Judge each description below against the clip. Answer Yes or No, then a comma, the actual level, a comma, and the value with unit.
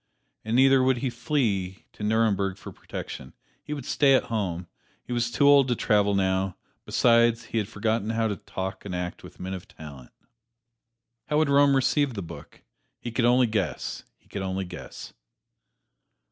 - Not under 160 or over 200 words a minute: Yes, average, 175 wpm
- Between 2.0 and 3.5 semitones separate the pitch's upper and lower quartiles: No, average, 4.8 semitones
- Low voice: Yes, low, 110 Hz